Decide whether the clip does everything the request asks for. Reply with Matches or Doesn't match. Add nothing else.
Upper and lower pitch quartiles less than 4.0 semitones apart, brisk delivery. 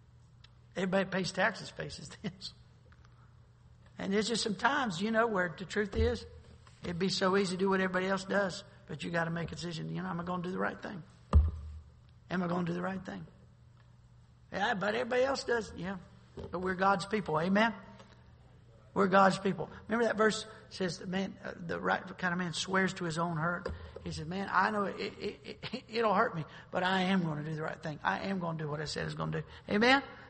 Matches